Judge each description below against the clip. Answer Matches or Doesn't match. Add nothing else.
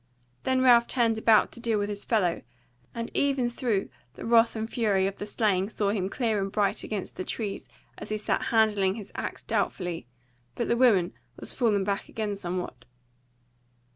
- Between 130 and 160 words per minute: Doesn't match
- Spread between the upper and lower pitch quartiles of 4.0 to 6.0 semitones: Doesn't match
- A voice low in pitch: Doesn't match